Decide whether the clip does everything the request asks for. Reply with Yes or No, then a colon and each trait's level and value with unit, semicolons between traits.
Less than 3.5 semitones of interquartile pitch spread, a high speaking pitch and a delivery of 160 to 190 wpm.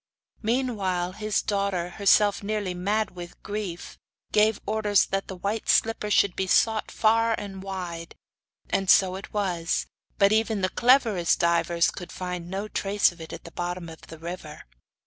Yes: average, 3.1 semitones; high, 195 Hz; average, 165 wpm